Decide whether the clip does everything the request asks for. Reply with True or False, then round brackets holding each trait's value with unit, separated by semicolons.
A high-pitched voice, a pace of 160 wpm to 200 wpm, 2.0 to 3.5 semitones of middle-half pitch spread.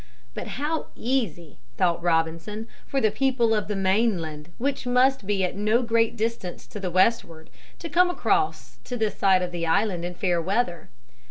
False (205 Hz; 175 wpm; 5.2 semitones)